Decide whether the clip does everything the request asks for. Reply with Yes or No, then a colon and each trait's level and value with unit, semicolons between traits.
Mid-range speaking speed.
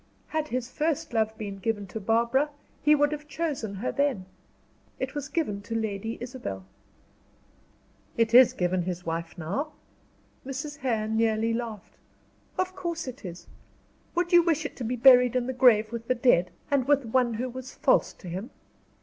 Yes: average, 175 wpm